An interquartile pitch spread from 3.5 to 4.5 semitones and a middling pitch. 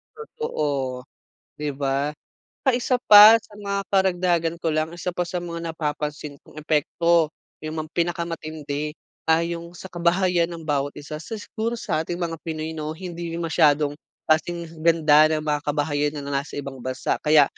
No: average, 2.7 semitones; medium, 160 Hz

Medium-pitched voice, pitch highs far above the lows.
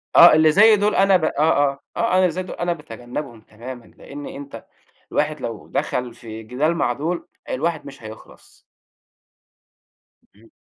Yes: medium, 145 Hz; wide, 6.0 semitones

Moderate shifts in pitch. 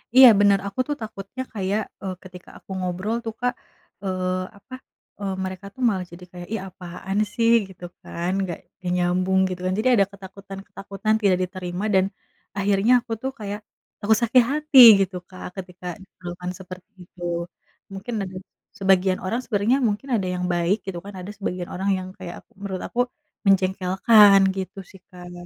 No: narrow, 2.1 semitones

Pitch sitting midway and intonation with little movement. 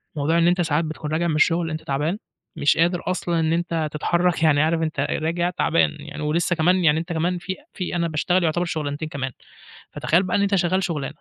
Yes: medium, 165 Hz; narrow, 2.1 semitones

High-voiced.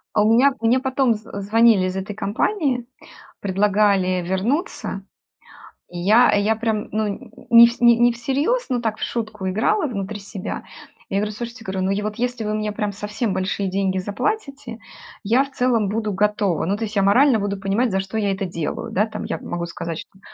Yes: high, 215 Hz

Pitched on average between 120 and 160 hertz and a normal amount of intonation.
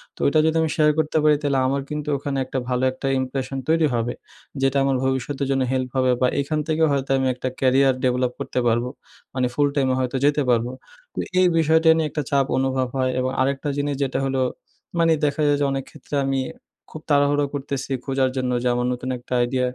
No: low, 135 Hz; narrow, 2.0 semitones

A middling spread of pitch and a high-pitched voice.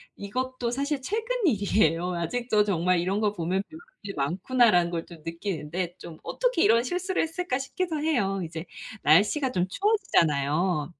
No: wide, 7.5 semitones; high, 200 Hz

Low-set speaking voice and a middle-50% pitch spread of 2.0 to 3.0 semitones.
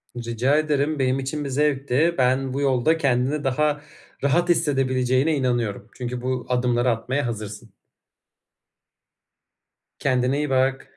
Yes: low, 130 Hz; narrow, 2.6 semitones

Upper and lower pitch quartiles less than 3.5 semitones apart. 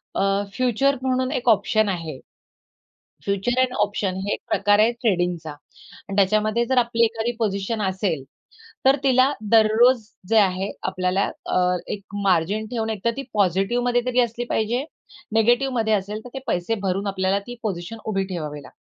No: average, 3.8 semitones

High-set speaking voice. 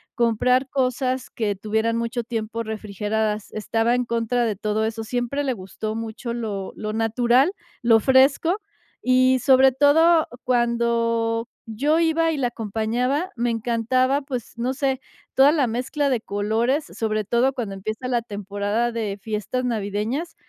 Yes: high, 235 Hz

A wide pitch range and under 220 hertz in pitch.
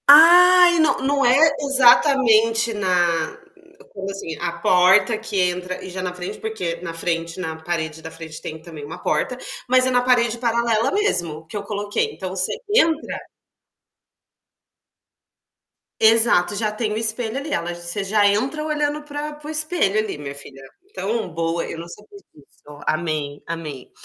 Yes: wide, 6.8 semitones; high, 205 Hz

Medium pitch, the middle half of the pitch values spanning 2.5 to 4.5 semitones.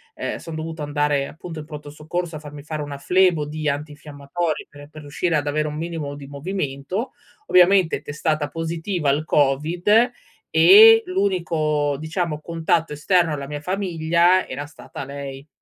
Yes: medium, 155 Hz; average, 2.9 semitones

